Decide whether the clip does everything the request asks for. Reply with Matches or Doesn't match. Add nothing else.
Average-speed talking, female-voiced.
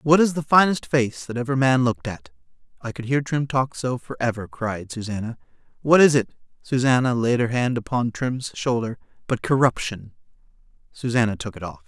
Doesn't match